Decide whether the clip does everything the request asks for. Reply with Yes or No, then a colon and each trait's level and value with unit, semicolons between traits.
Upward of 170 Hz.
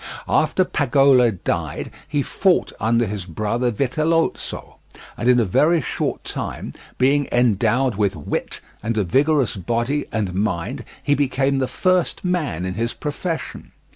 No: low, 125 Hz